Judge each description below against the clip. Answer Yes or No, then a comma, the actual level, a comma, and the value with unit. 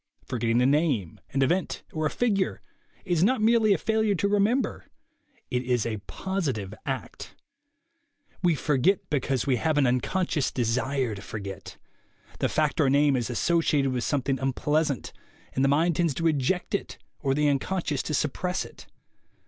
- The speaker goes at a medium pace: Yes, average, 165 wpm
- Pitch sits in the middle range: Yes, medium, 145 Hz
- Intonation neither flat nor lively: No, wide, 5.7 semitones